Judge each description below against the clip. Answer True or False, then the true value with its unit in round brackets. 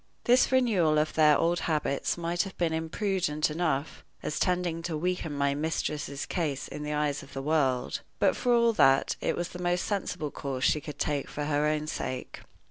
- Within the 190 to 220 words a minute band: True (195 wpm)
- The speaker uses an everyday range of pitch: True (3.1 semitones)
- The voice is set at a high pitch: False (155 Hz)